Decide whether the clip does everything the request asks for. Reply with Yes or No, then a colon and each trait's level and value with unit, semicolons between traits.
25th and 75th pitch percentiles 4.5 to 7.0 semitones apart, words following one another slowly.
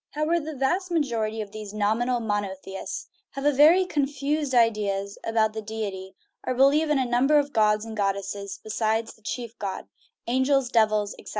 No: average, 4.8 semitones; average, 170 wpm